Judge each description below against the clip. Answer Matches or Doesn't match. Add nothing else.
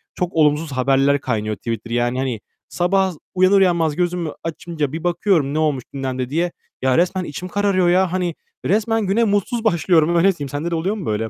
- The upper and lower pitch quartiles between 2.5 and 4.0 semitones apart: Doesn't match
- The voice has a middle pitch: Matches